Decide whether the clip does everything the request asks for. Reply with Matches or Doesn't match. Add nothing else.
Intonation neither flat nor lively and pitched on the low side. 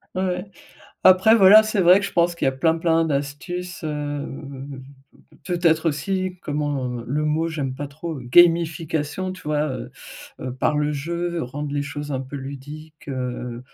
Doesn't match